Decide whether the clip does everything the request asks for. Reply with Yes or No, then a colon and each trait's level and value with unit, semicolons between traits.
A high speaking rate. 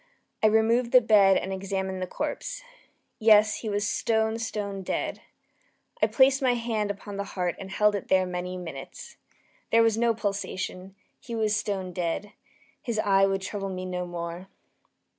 No: average, 165 wpm